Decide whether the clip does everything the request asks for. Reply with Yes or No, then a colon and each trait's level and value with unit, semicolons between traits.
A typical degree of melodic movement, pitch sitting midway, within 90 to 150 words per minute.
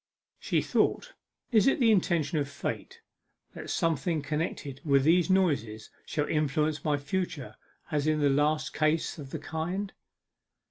Yes: average, 3.3 semitones; medium, 155 Hz; average, 145 wpm